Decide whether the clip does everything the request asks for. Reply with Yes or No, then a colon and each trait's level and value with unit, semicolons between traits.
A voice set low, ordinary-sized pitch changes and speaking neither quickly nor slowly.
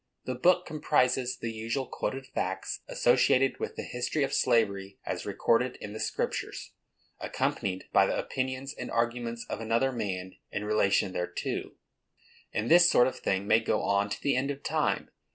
Yes: low, 115 Hz; average, 4.3 semitones; average, 170 wpm